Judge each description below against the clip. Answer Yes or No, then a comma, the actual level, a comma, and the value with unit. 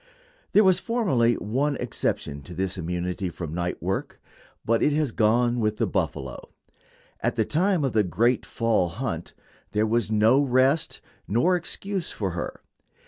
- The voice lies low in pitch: Yes, low, 115 Hz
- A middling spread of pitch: No, wide, 6.9 semitones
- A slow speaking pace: No, average, 155 wpm